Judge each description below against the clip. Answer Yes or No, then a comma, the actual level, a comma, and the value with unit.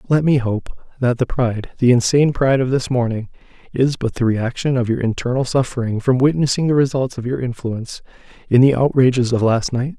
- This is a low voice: Yes, low, 125 Hz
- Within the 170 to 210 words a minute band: Yes, average, 200 wpm